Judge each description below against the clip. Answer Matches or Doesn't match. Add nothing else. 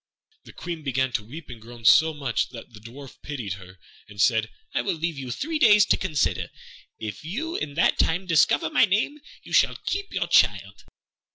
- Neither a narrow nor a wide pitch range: Doesn't match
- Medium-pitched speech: Matches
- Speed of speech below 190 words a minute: Doesn't match